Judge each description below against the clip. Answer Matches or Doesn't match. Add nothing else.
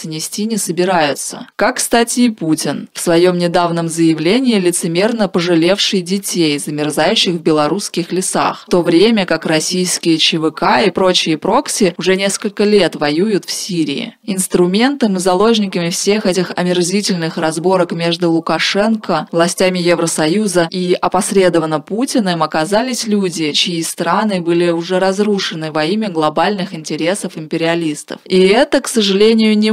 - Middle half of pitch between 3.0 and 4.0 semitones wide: Matches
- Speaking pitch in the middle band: Matches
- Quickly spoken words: Doesn't match